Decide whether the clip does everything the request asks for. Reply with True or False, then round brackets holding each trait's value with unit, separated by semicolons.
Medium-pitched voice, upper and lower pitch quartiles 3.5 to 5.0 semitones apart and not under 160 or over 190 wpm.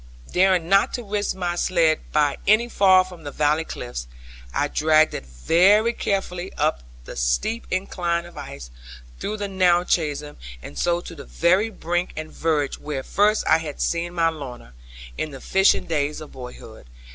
True (170 Hz; 4.1 semitones; 170 wpm)